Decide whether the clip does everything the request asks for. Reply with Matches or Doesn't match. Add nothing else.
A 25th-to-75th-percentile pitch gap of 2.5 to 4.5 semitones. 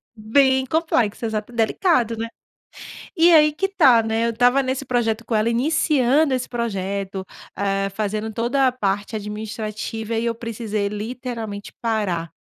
Matches